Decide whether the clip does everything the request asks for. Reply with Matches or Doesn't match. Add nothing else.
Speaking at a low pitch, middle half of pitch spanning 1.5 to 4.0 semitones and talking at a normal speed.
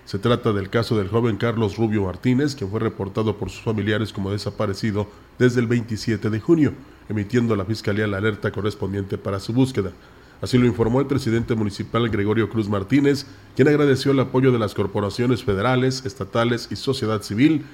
Matches